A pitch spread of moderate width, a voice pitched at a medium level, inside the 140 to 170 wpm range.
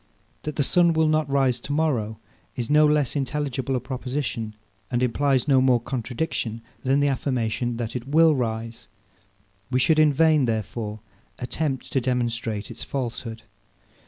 No: average, 3.7 semitones; low, 130 Hz; average, 155 wpm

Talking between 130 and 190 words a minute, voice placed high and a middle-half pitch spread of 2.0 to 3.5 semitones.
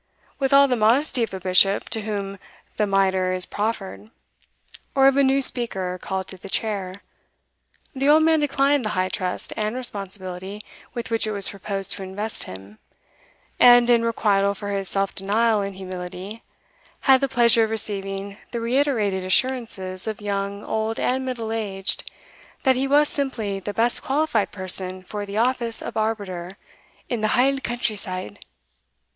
No: average, 165 wpm; high, 210 Hz; average, 3.9 semitones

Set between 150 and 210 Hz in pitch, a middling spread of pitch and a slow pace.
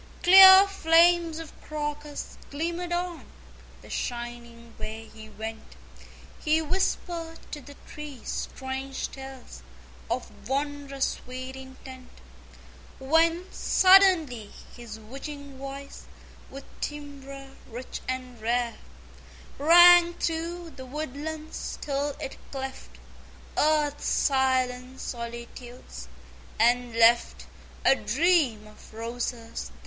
No: very high, 275 Hz; average, 4.5 semitones; slow, 100 wpm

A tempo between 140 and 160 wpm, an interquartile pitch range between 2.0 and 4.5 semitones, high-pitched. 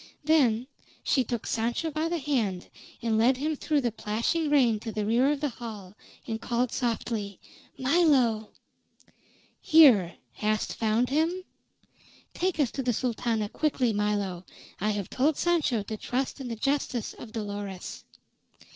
No: average, 145 wpm; average, 4.9 semitones; high, 240 Hz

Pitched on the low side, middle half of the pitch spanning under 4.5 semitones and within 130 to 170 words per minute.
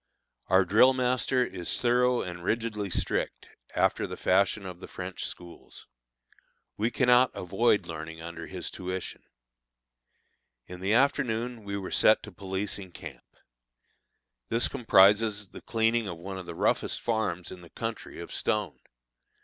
Yes: low, 100 Hz; average, 4.1 semitones; average, 140 wpm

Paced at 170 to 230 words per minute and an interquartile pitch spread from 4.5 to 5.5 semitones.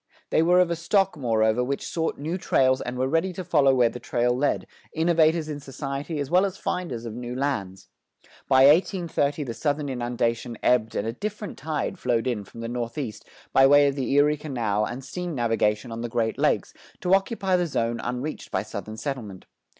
Yes: average, 195 wpm; average, 5.2 semitones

